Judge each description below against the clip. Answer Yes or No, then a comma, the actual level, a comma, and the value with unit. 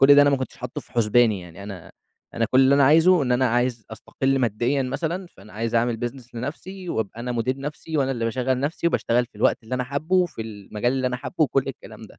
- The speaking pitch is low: Yes, low, 125 Hz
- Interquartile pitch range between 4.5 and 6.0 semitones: No, average, 3.4 semitones